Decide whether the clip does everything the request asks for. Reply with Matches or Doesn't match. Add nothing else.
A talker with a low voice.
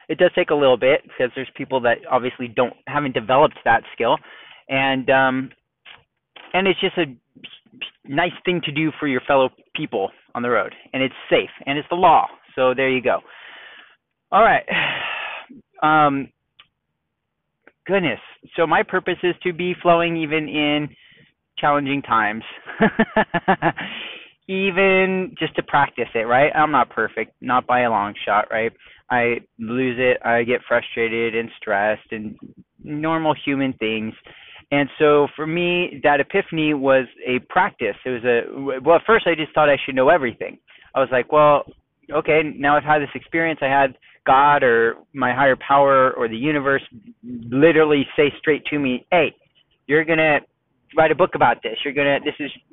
Doesn't match